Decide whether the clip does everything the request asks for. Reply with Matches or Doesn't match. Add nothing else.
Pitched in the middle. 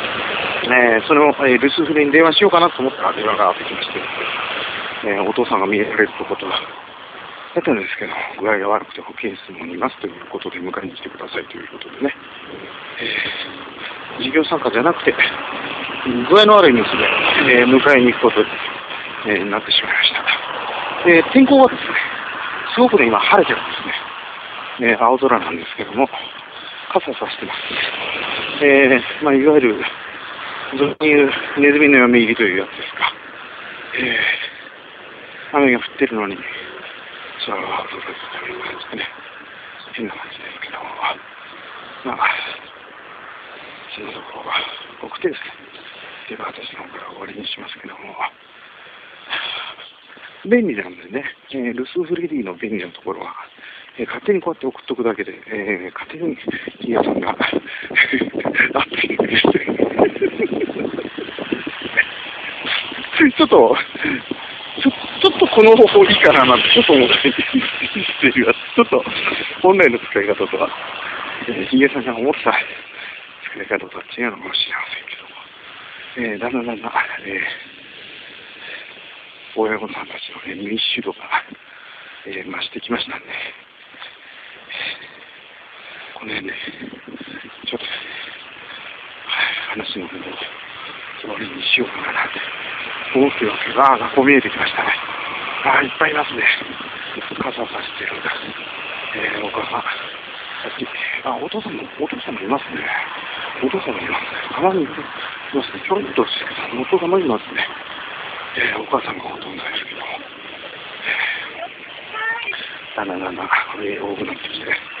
Matches